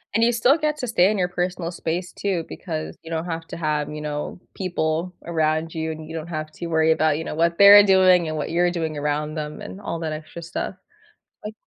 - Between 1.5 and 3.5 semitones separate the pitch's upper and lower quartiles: Yes, average, 2.7 semitones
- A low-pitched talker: No, medium, 165 Hz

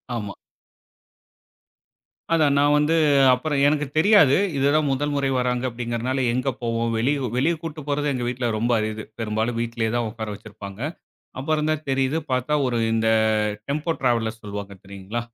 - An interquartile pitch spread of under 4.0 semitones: No, average, 4.4 semitones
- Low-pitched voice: Yes, low, 125 Hz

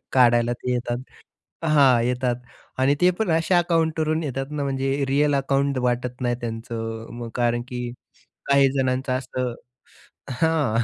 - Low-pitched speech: Yes, low, 130 Hz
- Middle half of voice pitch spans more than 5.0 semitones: No, average, 2.8 semitones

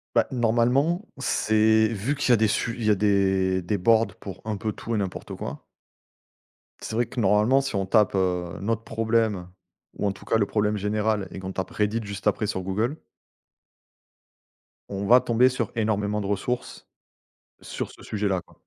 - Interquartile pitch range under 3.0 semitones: Yes, narrow, 2.6 semitones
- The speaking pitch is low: Yes, low, 105 Hz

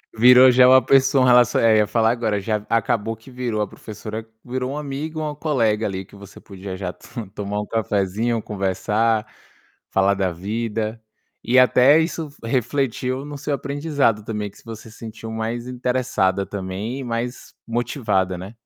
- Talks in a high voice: No, low, 115 Hz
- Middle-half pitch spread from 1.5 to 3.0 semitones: No, average, 3.4 semitones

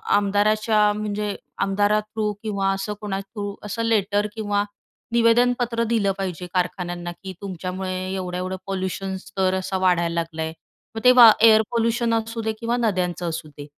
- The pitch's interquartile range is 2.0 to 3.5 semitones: Yes, average, 3.0 semitones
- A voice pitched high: Yes, high, 205 Hz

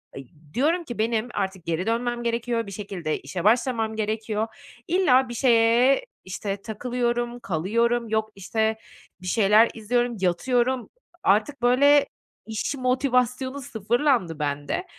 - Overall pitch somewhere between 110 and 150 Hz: No, high, 230 Hz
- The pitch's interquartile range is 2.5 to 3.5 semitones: Yes, average, 3.2 semitones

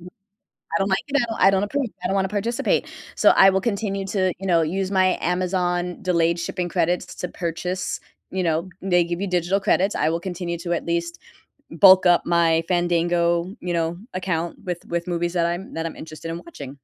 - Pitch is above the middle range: No, medium, 175 Hz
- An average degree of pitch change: No, narrow, 2.0 semitones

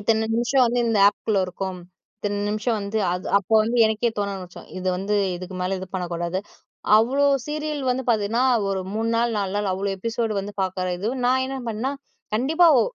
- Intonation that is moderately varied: Yes, average, 3.7 semitones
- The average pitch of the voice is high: Yes, high, 215 Hz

